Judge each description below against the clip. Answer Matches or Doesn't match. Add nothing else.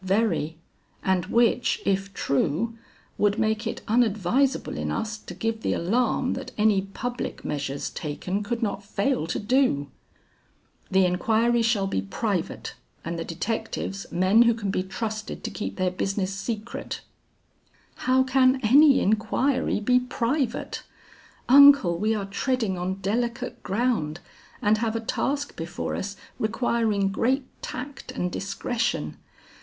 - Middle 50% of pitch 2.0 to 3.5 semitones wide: Doesn't match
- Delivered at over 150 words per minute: Doesn't match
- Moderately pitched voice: Doesn't match